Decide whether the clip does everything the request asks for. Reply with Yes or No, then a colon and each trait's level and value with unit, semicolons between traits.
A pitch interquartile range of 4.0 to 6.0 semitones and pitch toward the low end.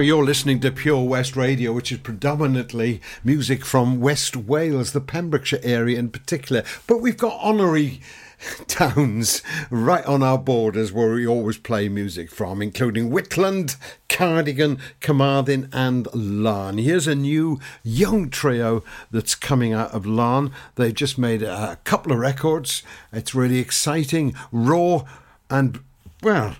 Yes: average, 4.3 semitones; low, 130 Hz